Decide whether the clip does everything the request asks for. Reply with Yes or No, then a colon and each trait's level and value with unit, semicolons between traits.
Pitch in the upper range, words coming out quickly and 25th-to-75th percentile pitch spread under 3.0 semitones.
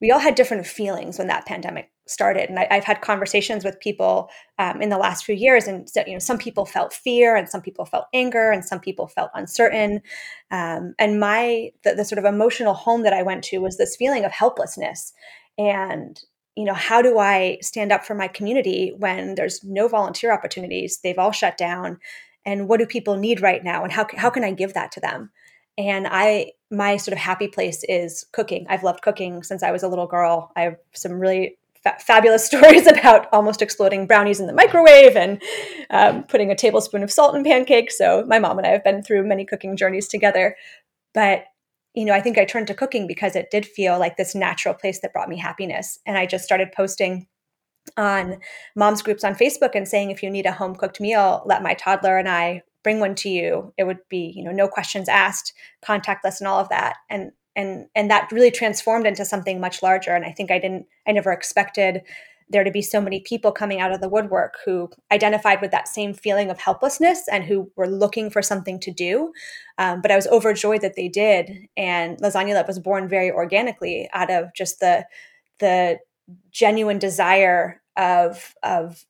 Yes: high, 200 Hz; fast, 210 wpm; narrow, 2.5 semitones